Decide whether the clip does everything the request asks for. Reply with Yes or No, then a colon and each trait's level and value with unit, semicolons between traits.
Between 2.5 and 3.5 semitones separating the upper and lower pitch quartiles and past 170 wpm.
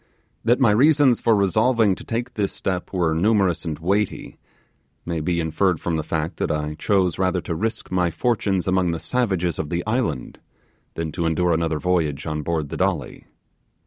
No: average, 4.6 semitones; average, 180 wpm